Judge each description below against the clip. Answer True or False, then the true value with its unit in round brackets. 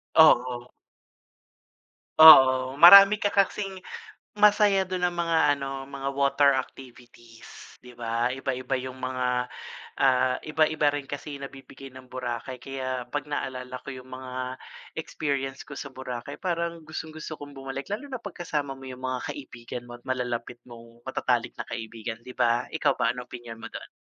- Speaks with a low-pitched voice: True (130 Hz)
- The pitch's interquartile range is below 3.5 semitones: True (2.9 semitones)